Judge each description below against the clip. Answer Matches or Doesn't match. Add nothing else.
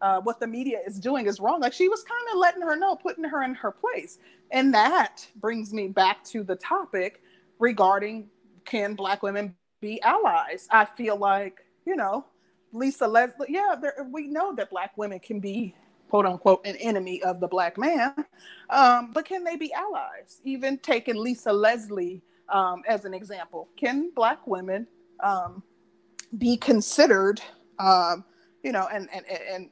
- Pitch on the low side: Doesn't match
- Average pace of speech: Matches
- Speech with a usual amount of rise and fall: Doesn't match